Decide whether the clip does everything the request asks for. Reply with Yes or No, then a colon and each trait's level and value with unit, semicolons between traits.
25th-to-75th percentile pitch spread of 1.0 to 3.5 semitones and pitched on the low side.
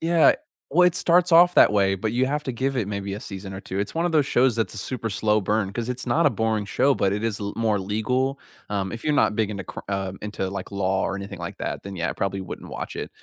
No: average, 4.9 semitones; low, 105 Hz